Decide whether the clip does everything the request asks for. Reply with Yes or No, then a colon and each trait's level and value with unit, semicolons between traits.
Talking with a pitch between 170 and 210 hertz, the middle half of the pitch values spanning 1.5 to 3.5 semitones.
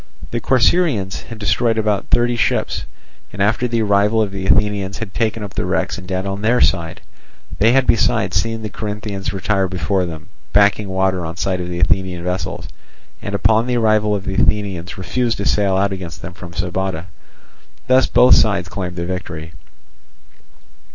No: low, 100 Hz; average, 2.9 semitones